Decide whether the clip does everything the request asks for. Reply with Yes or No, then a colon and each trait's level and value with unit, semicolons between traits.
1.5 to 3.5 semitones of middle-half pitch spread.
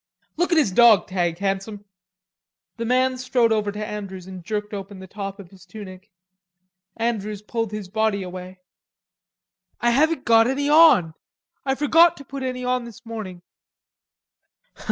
No: average, 4.5 semitones